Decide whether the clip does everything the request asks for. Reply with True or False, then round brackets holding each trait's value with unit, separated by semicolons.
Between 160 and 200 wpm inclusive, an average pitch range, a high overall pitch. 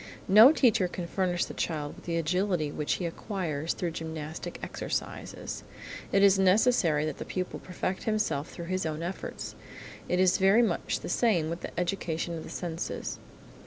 False (170 wpm; 3.1 semitones; 180 Hz)